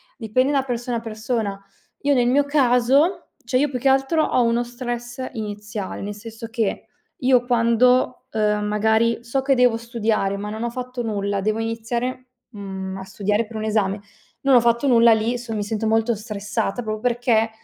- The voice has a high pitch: Yes, high, 230 Hz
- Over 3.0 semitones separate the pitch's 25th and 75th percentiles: No, average, 2.7 semitones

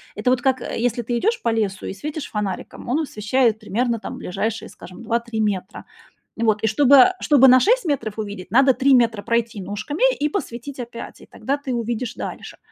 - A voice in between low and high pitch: No, high, 235 Hz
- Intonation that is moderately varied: Yes, average, 3.7 semitones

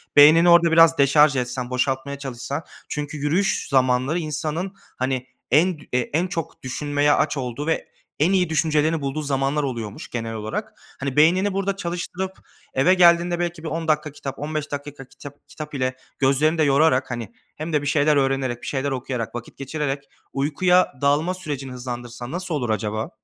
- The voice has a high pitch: No, medium, 145 Hz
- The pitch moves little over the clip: No, average, 3.5 semitones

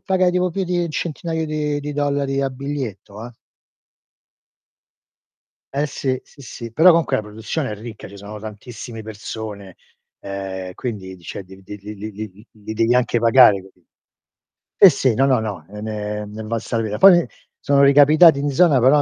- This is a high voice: No, low, 120 Hz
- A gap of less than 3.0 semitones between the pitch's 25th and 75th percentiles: No, wide, 5.5 semitones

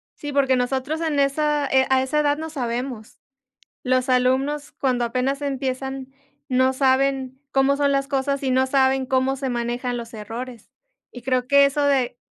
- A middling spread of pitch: No, narrow, 1.6 semitones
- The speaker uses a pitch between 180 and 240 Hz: No, very high, 265 Hz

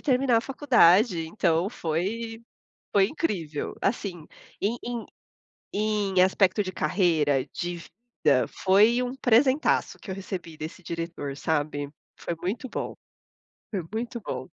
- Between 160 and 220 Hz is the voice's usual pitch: Yes, high, 190 Hz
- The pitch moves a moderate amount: No, wide, 5.8 semitones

